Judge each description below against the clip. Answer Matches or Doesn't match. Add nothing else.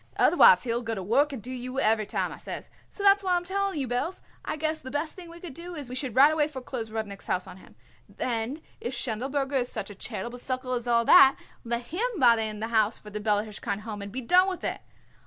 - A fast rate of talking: Matches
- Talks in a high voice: Matches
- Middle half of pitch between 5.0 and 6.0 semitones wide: Matches